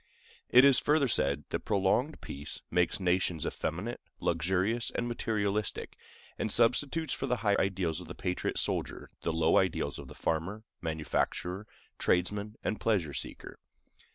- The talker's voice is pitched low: Yes, very low, 95 Hz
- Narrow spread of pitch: No, average, 4.7 semitones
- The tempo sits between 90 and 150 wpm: Yes, average, 145 wpm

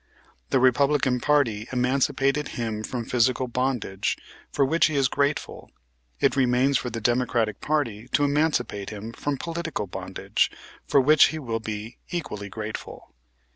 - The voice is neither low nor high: No, low, 125 Hz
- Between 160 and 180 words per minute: No, average, 140 wpm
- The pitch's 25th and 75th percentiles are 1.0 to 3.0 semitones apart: No, average, 4.1 semitones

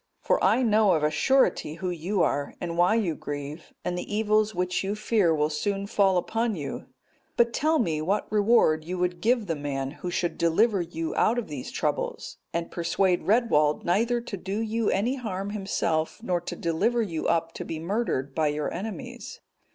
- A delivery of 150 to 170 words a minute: No, average, 190 wpm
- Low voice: No, medium, 185 Hz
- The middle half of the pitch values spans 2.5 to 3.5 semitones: No, average, 4.9 semitones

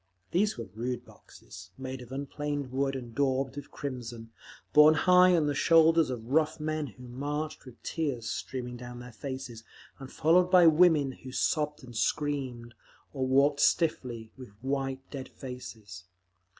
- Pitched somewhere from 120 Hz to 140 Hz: Yes, low, 135 Hz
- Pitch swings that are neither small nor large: Yes, average, 3.4 semitones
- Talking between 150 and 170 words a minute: Yes, average, 155 wpm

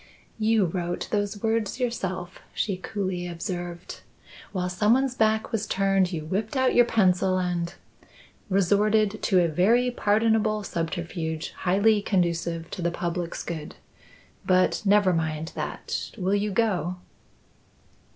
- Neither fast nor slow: No, slow, 130 wpm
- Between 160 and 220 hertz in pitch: Yes, high, 190 Hz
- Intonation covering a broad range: No, average, 3.5 semitones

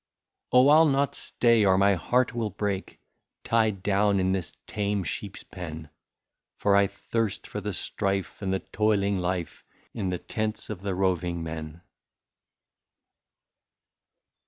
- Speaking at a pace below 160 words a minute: Yes, average, 140 wpm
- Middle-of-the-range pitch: No, low, 100 Hz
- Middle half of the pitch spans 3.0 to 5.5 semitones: No, narrow, 2.6 semitones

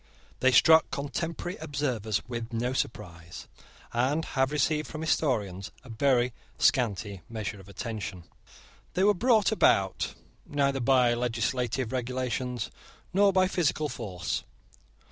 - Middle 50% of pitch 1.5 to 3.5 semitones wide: No, average, 4.9 semitones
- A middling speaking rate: No, slow, 120 wpm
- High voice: No, low, 125 Hz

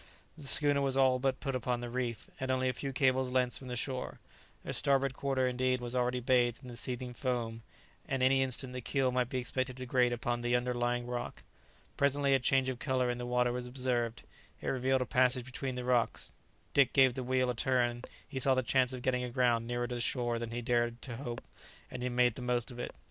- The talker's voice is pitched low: Yes, low, 125 Hz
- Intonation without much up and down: Yes, narrow, 1.3 semitones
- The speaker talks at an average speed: No, fast, 235 wpm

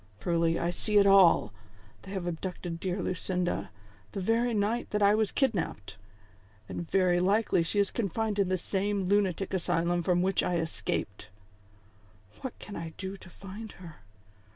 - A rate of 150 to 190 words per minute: Yes, average, 170 wpm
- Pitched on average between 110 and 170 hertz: No, medium, 185 Hz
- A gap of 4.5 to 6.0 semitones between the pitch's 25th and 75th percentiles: No, average, 3.0 semitones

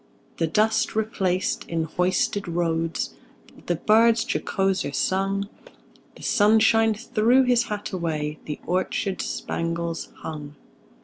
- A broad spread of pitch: No, average, 4.5 semitones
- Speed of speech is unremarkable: No, slow, 110 wpm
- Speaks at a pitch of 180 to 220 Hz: Yes, high, 190 Hz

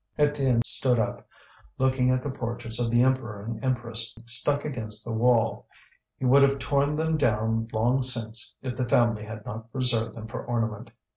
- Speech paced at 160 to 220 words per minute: Yes, average, 175 wpm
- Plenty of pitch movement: No, narrow, 2.6 semitones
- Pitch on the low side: Yes, low, 120 Hz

